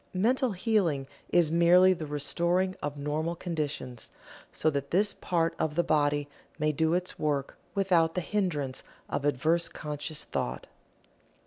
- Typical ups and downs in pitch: Yes, average, 3.5 semitones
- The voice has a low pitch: No, medium, 160 Hz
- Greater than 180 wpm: No, average, 140 wpm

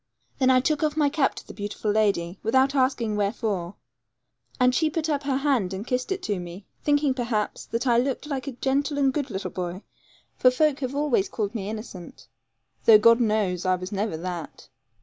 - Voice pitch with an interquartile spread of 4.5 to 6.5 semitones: Yes, average, 5.3 semitones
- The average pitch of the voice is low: No, high, 240 Hz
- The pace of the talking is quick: No, average, 195 wpm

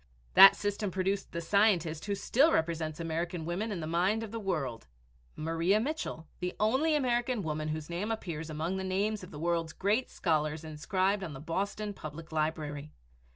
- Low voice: No, medium, 175 Hz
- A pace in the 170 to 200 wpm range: Yes, average, 175 wpm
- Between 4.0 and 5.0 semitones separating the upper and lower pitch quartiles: Yes, average, 4.5 semitones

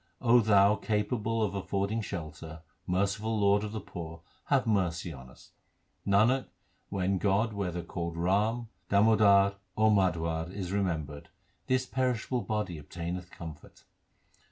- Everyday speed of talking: No, slow, 130 wpm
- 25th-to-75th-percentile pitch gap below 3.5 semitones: No, average, 4.0 semitones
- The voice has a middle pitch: No, low, 100 Hz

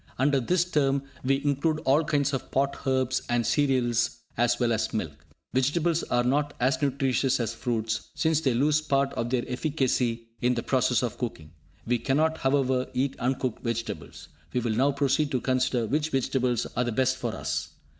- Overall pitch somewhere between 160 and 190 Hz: No, low, 130 Hz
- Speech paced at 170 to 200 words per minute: Yes, average, 180 wpm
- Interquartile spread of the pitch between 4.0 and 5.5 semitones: No, average, 2.7 semitones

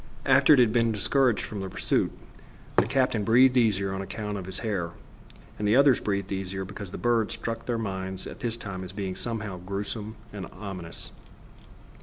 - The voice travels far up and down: No, average, 3.2 semitones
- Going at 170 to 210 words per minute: Yes, average, 180 wpm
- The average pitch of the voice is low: Yes, low, 105 Hz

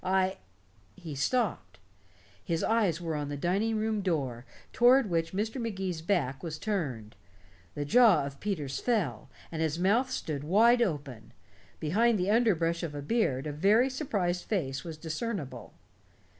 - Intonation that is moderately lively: No, wide, 6.8 semitones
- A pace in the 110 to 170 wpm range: Yes, average, 150 wpm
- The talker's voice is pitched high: No, medium, 175 Hz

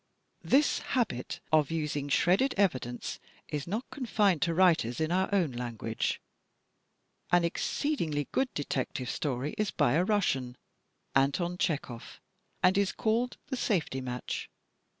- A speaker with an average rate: No, slow, 130 wpm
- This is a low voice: No, medium, 165 Hz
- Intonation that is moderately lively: No, wide, 6.9 semitones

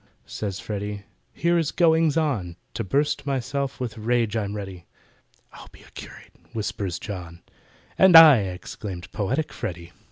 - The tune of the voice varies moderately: No, wide, 6.8 semitones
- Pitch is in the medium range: No, low, 110 Hz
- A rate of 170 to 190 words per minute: No, average, 140 wpm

